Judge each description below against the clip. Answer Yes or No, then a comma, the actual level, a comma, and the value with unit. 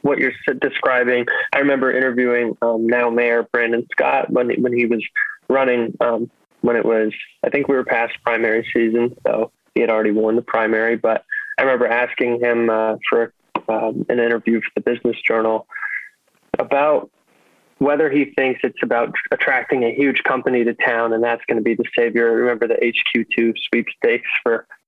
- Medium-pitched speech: No, low, 120 Hz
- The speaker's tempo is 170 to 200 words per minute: Yes, average, 180 wpm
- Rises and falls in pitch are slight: Yes, narrow, 2.1 semitones